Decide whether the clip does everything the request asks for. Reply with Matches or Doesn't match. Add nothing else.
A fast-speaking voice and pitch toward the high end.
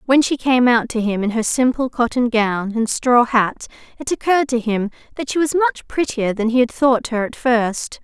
Matches